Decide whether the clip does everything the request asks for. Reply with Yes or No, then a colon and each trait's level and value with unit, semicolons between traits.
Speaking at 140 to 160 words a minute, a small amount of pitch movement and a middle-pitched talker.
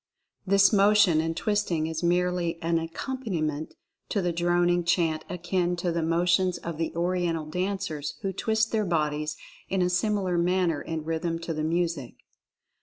Yes: average, 155 wpm; narrow, 2.2 semitones; medium, 175 Hz